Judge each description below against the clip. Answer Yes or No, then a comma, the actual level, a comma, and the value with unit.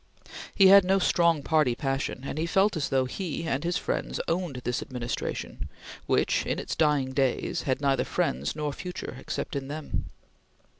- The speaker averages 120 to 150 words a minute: No, average, 170 wpm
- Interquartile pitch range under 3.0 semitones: No, average, 4.2 semitones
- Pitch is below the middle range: No, medium, 145 Hz